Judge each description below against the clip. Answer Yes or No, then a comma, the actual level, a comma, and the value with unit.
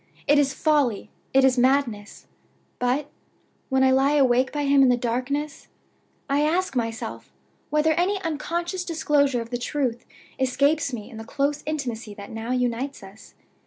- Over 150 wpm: Yes, average, 160 wpm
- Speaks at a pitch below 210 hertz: No, very high, 270 Hz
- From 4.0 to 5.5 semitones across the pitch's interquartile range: No, average, 3.4 semitones